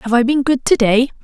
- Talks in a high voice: Yes, very high, 250 Hz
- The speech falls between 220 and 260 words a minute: Yes, fast, 245 wpm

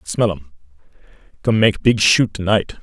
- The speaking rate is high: No, average, 150 wpm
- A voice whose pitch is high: No, low, 100 Hz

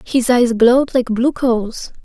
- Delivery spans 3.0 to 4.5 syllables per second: Yes, 4.3 syllables/s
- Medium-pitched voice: No, high, 245 Hz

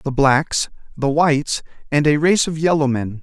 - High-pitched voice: No, medium, 145 Hz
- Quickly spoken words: No, average, 185 wpm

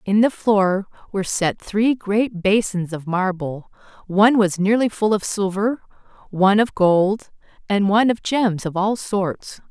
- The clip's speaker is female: Yes, female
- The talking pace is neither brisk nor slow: Yes, average, 160 wpm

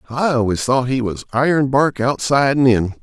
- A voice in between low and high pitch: No, low, 130 Hz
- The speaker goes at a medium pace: Yes, average, 180 wpm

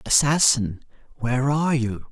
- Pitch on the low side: Yes, low, 130 Hz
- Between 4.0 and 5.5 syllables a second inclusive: Yes, 5.1 syllables/s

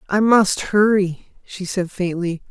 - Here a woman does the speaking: Yes, female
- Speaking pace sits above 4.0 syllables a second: No, 3.7 syllables/s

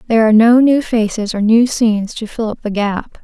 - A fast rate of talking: Yes, fast, 240 wpm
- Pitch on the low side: No, high, 225 Hz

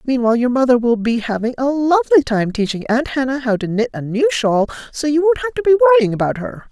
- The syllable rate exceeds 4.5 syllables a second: Yes, 6.3 syllables/s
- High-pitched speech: Yes, very high, 255 Hz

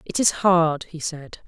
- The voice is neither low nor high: Yes, medium, 165 Hz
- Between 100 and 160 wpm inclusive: No, fast, 205 wpm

